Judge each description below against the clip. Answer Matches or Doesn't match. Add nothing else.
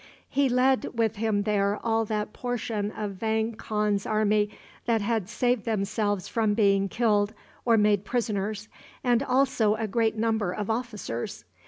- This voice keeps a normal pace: Matches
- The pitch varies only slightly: Matches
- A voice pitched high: Matches